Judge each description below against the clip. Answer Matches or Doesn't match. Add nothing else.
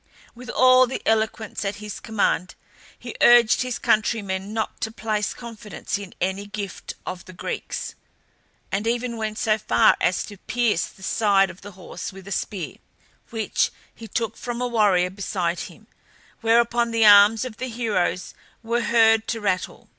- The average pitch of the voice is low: Doesn't match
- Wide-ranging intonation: Doesn't match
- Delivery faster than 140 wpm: Matches